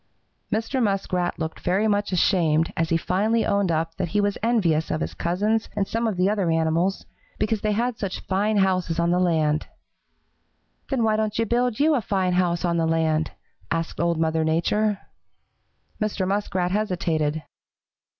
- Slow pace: No, average, 170 wpm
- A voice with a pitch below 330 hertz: Yes, medium, 185 Hz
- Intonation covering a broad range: No, average, 4.4 semitones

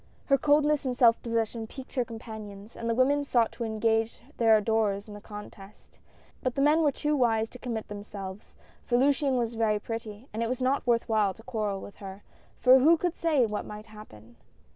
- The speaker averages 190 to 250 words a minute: Yes, fast, 205 wpm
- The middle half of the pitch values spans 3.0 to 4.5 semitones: Yes, average, 3.4 semitones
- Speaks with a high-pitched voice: Yes, high, 230 Hz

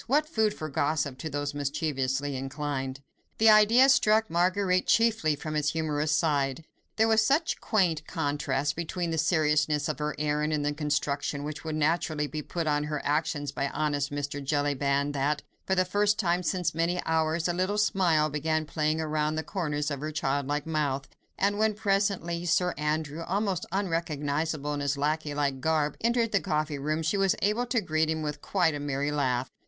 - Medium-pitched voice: Yes, medium, 155 Hz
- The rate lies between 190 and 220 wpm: No, average, 180 wpm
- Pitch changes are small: No, average, 3.6 semitones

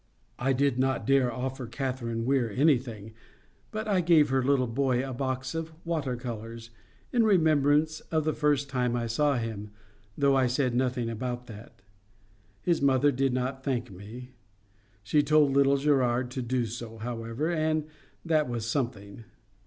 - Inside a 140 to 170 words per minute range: Yes, average, 160 wpm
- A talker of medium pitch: No, low, 130 Hz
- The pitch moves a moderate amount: Yes, average, 3.2 semitones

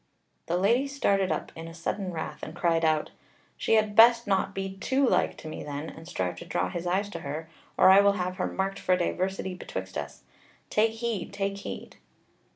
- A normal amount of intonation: Yes, average, 3.5 semitones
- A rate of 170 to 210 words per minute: Yes, average, 200 wpm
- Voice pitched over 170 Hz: Yes, high, 190 Hz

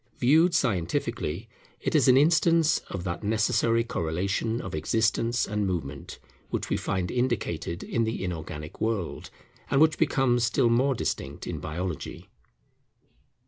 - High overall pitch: No, low, 110 Hz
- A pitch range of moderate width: No, wide, 6.2 semitones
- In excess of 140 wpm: No, slow, 135 wpm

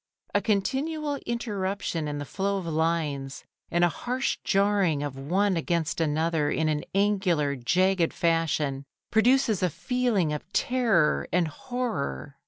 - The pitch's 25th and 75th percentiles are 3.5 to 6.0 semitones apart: Yes, average, 5.3 semitones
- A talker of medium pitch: Yes, medium, 175 Hz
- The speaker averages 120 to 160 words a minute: Yes, slow, 135 wpm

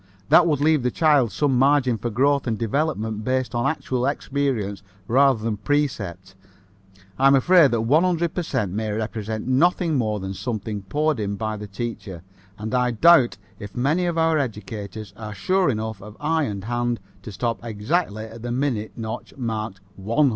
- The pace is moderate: Yes, average, 175 wpm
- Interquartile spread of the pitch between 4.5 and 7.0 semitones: Yes, average, 5.0 semitones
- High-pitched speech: No, low, 120 Hz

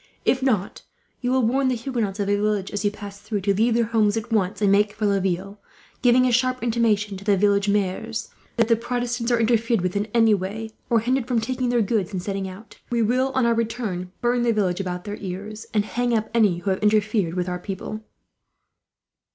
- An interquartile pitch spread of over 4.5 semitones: No, average, 3.0 semitones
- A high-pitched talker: Yes, high, 215 Hz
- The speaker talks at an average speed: No, fast, 225 wpm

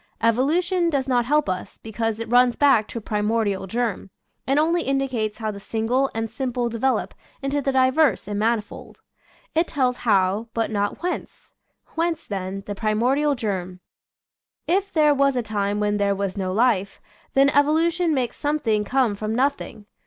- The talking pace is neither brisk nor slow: Yes, average, 175 wpm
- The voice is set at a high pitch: Yes, high, 235 Hz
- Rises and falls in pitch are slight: No, average, 4.9 semitones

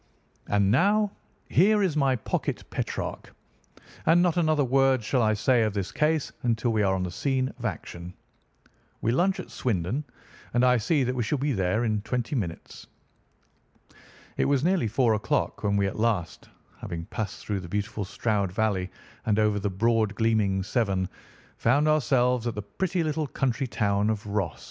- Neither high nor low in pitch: No, low, 115 Hz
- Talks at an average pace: Yes, average, 175 wpm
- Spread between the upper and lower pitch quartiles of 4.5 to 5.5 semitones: Yes, average, 4.9 semitones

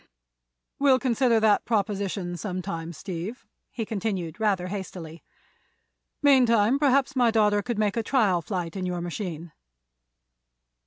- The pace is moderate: No, slow, 125 wpm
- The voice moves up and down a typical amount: Yes, average, 4.5 semitones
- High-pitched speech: Yes, high, 205 Hz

